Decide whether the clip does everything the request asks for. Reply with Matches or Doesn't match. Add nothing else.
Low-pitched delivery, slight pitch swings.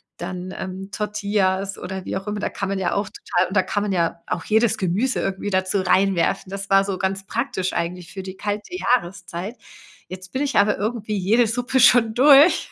Doesn't match